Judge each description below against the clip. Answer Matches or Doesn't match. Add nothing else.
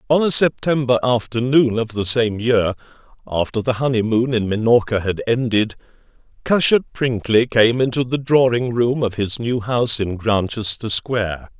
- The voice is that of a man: Matches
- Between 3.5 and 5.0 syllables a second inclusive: Matches